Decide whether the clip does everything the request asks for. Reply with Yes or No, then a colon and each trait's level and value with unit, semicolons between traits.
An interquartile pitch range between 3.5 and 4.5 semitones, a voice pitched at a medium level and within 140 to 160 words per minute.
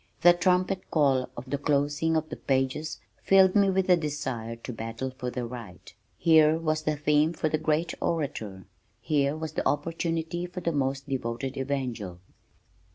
Yes: average, 3.9 semitones; medium, 150 Hz; average, 155 wpm